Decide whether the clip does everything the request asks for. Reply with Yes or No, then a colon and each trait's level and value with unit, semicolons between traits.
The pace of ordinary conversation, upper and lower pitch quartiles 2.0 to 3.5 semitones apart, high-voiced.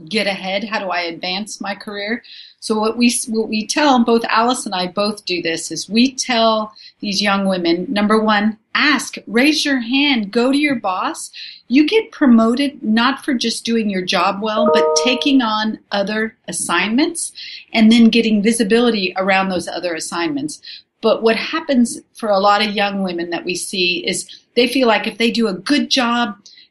No: average, 185 wpm; average, 3.9 semitones; high, 220 Hz